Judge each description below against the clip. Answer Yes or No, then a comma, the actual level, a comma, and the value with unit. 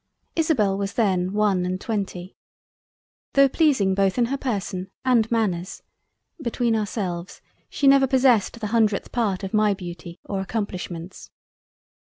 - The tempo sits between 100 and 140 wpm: Yes, slow, 135 wpm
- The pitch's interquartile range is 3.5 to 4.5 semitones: Yes, average, 4.0 semitones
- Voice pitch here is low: No, high, 205 Hz